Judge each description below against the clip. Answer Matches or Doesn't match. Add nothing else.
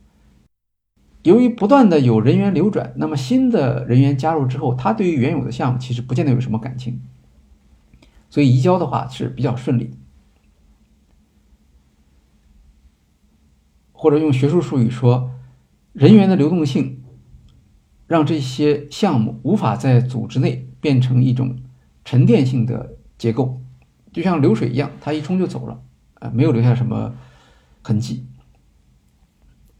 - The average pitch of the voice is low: Matches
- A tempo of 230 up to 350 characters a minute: Doesn't match